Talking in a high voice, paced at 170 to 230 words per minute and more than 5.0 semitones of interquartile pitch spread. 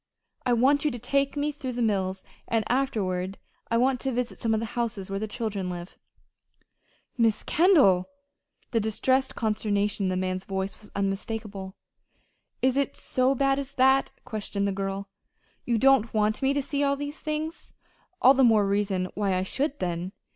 Yes: high, 225 Hz; average, 175 wpm; wide, 5.4 semitones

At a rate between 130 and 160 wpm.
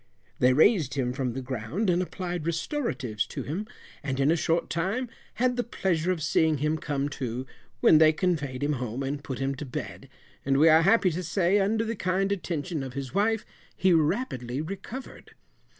No: average, 190 wpm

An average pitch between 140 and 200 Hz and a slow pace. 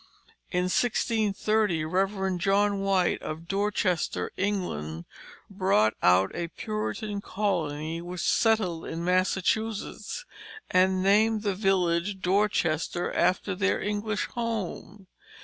Yes: high, 190 Hz; slow, 100 wpm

